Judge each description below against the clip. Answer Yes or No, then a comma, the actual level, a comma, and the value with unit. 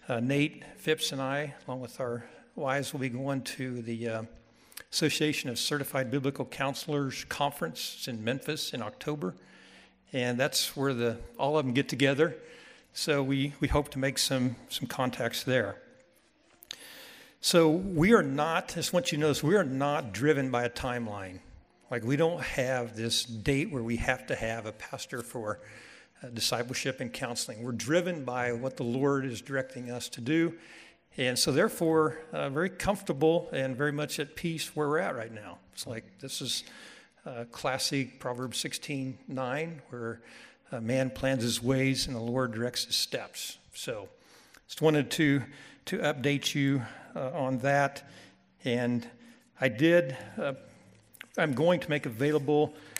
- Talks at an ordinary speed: Yes, average, 170 wpm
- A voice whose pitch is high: No, low, 135 Hz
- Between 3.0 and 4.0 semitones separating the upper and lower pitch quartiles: Yes, average, 3.5 semitones